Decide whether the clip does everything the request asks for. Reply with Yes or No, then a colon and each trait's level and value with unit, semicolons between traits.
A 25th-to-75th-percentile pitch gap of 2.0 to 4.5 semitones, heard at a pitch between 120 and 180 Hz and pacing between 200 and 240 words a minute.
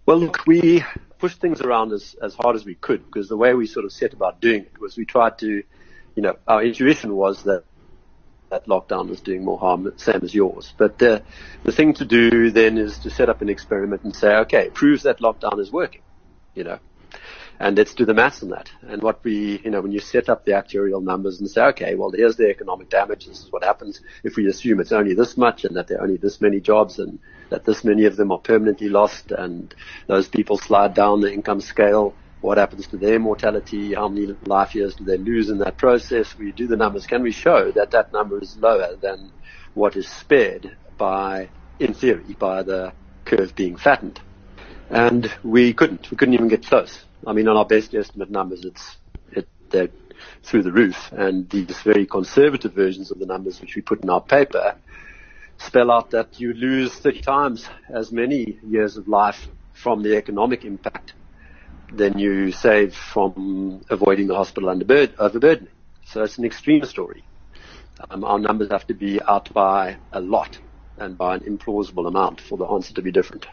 No: average, 3.1 semitones; low, 105 Hz; fast, 205 wpm